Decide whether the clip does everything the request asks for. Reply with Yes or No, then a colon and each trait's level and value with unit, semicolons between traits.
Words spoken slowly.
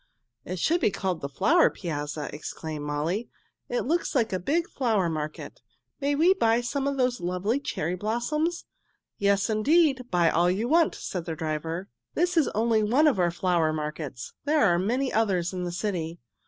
No: average, 180 wpm